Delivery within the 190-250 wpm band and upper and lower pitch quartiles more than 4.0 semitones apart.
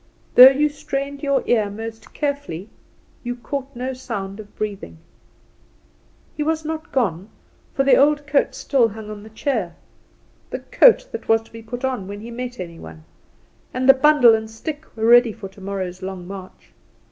No: average, 175 wpm; wide, 5.4 semitones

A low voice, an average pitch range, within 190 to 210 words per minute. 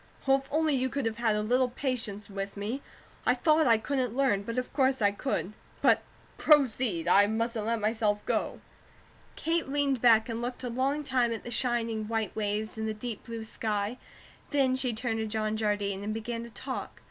No: high, 230 Hz; average, 3.3 semitones; average, 200 wpm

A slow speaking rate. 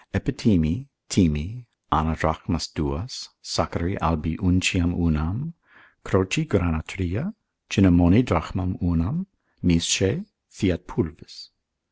Yes: slow, 90 wpm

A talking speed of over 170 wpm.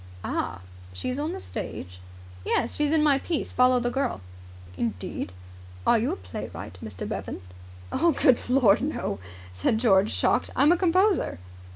No: average, 155 wpm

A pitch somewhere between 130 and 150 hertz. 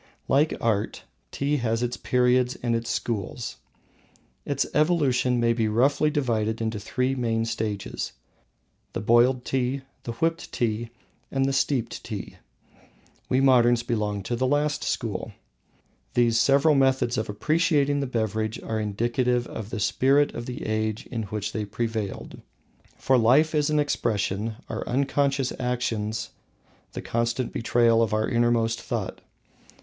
No: low, 120 Hz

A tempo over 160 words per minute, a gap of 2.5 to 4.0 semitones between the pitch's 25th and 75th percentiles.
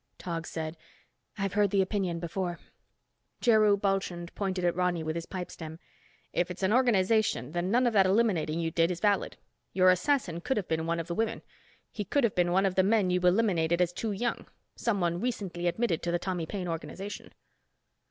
Yes: average, 190 wpm; average, 3.1 semitones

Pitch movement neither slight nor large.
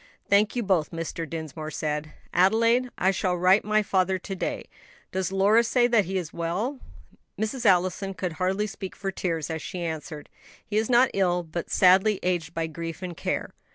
Yes: average, 3.9 semitones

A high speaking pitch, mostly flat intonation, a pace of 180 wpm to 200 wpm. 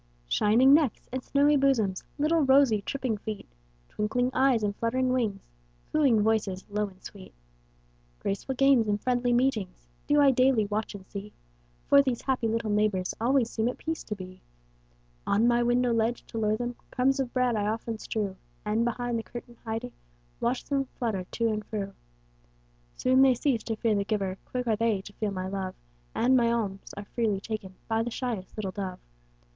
No: high, 230 Hz; average, 3.5 semitones; average, 185 wpm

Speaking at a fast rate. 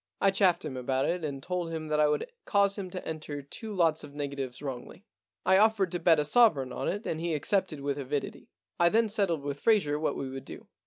Yes: fast, 230 wpm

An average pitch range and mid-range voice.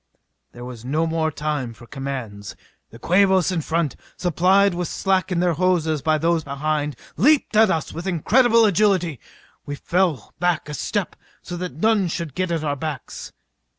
Yes: average, 4.1 semitones; medium, 165 Hz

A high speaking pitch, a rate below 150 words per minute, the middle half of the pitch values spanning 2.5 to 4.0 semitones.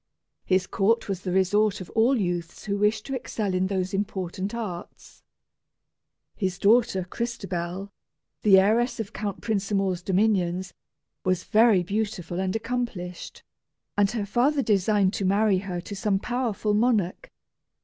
Yes: high, 200 Hz; average, 140 wpm; average, 2.8 semitones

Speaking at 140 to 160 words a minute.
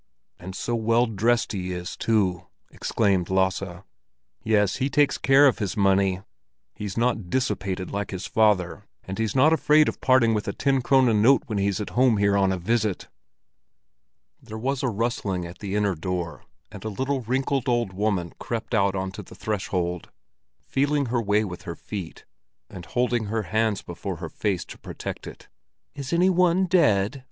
No: average, 175 wpm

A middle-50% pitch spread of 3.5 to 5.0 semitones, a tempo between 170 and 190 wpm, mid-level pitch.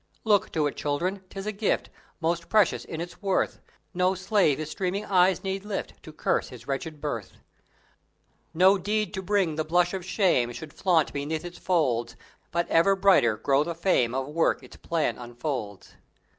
Yes: average, 4.5 semitones; average, 175 wpm; medium, 170 Hz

